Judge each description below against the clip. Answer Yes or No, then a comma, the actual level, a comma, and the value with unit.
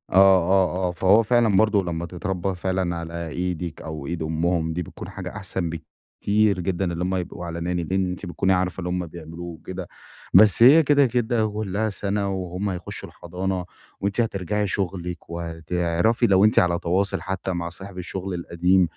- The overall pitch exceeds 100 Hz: No, very low, 90 Hz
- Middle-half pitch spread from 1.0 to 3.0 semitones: Yes, narrow, 2.4 semitones